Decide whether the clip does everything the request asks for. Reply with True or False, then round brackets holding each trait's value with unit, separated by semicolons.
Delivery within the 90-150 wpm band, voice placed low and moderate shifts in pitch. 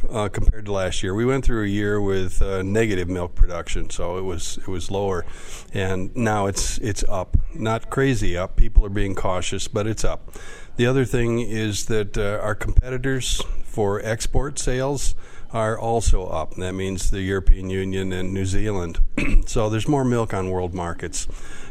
False (180 wpm; 100 Hz; 3.2 semitones)